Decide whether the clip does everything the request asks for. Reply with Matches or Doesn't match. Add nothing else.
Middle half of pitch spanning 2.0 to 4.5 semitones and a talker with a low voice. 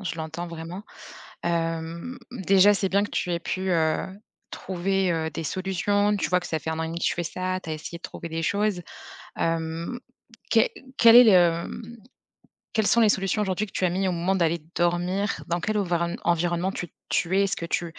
Doesn't match